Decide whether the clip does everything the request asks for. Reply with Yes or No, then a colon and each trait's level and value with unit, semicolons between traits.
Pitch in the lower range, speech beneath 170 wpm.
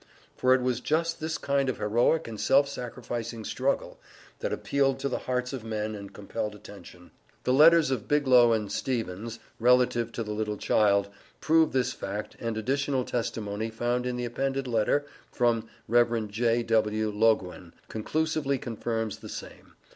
Yes: low, 120 Hz; average, 155 wpm